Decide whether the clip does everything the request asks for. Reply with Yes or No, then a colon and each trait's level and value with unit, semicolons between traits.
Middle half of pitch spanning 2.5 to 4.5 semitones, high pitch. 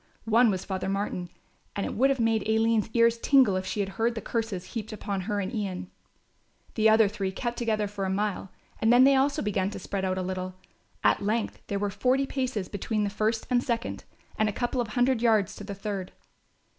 Yes: average, 3.0 semitones; high, 215 Hz